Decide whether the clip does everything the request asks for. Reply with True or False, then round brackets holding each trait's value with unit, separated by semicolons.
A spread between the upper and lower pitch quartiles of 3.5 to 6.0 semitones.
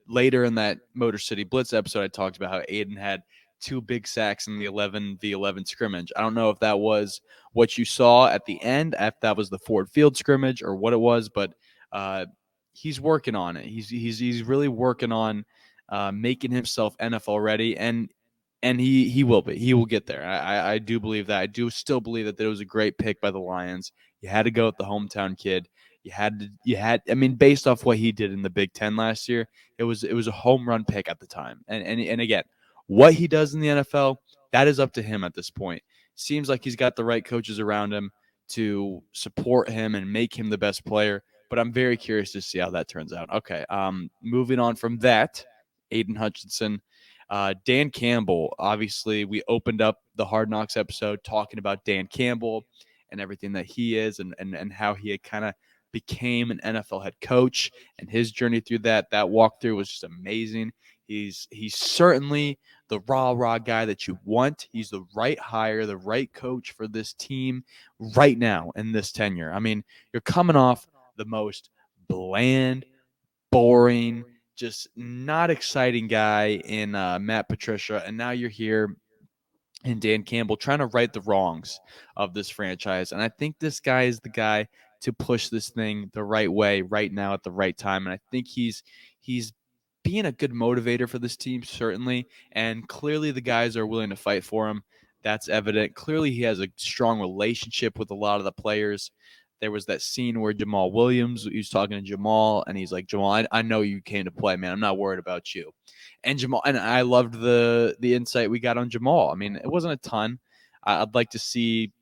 False (2.9 semitones)